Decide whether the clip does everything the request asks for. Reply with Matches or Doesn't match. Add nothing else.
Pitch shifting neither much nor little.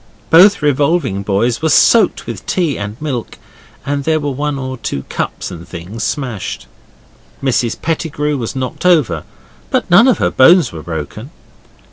Doesn't match